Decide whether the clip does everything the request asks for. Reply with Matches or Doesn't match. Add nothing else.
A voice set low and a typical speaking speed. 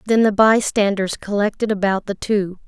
Doesn't match